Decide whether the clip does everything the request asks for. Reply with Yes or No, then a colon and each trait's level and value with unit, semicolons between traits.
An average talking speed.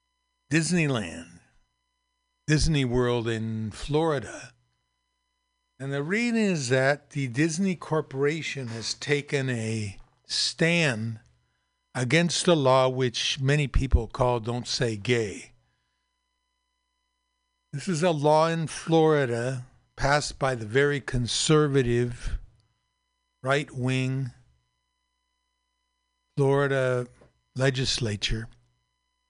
No: slow, 85 wpm